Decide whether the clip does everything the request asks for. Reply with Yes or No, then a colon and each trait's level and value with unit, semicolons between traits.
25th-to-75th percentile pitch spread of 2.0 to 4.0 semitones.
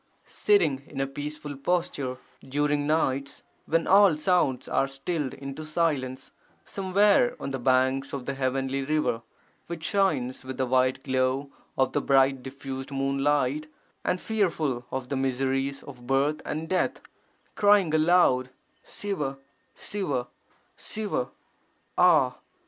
Yes: average, 3.1 semitones